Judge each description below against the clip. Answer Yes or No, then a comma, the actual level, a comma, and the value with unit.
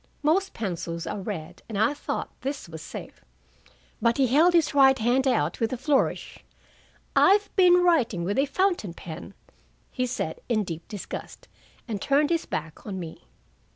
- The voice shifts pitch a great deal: Yes, wide, 7.9 semitones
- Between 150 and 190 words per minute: Yes, average, 165 wpm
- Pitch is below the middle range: No, high, 235 Hz